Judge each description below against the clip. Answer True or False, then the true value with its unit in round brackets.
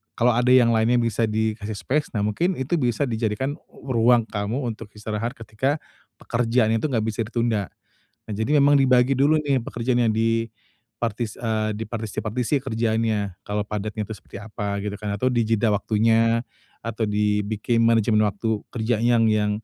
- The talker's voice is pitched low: True (115 Hz)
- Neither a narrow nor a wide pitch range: False (2.3 semitones)